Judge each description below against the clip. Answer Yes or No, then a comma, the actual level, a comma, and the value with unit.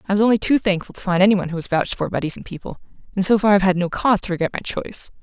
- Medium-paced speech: No, fast, 300 wpm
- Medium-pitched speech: No, high, 195 Hz